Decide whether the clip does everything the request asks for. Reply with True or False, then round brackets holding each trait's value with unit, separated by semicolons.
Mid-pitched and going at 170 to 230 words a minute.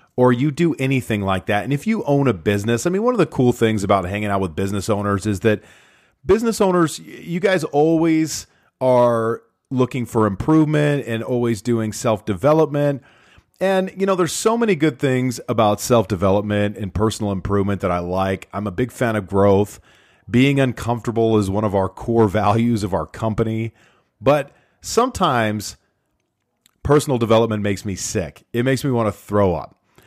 False (115 Hz; 175 wpm)